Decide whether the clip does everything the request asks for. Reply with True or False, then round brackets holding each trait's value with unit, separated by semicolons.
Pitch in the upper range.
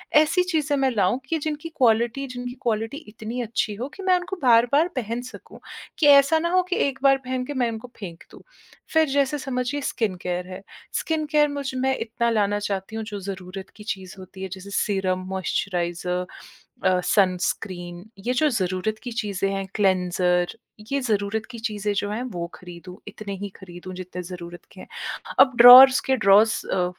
True (220 Hz)